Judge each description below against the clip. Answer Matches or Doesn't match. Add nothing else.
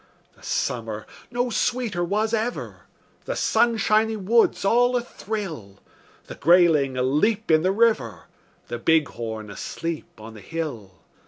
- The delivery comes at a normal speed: Doesn't match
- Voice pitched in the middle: Matches